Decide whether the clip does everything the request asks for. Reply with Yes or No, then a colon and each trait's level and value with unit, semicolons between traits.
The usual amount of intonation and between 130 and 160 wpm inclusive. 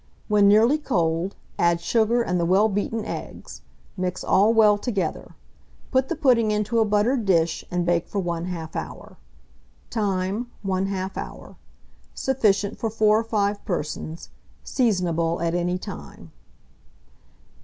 Yes: average, 3.9 semitones; slow, 135 wpm